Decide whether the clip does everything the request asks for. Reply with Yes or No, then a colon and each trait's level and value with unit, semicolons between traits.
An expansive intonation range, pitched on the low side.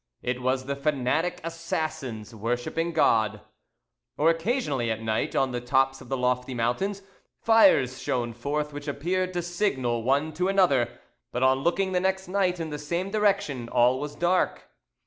No: wide, 6.0 semitones; medium, 145 Hz